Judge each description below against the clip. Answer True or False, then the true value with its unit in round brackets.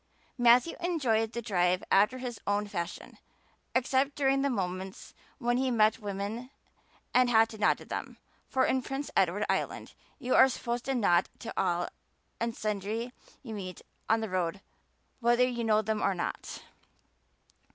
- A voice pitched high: True (225 Hz)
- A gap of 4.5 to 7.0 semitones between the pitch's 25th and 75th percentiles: False (4.0 semitones)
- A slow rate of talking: False (160 wpm)